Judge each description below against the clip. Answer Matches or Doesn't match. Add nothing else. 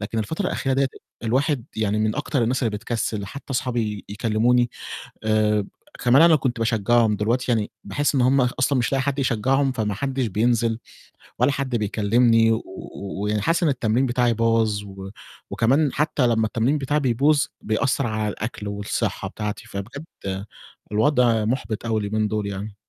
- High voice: Doesn't match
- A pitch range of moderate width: Matches